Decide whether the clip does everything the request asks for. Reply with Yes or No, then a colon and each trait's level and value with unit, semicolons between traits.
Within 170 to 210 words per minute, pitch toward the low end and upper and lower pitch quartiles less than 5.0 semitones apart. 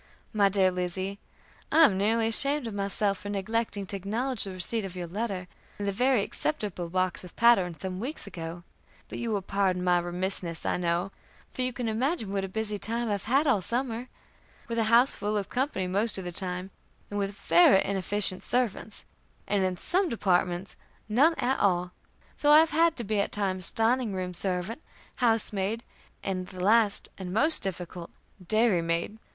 No: average, 185 wpm; high, 200 Hz; average, 3.9 semitones